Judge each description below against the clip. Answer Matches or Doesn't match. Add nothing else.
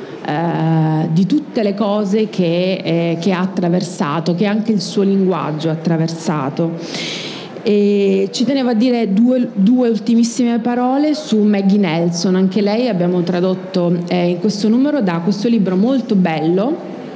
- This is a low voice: Doesn't match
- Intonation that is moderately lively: Matches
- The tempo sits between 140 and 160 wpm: Matches